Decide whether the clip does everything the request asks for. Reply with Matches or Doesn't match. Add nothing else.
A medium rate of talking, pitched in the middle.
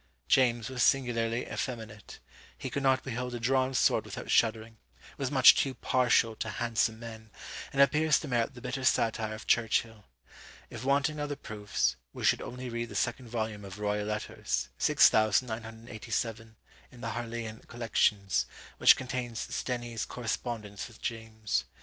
Doesn't match